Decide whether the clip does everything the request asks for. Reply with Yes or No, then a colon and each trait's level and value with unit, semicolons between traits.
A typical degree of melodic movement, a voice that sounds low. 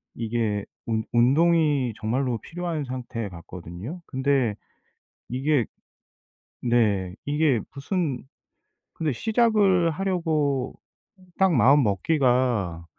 No: wide, 5.8 semitones; low, 130 Hz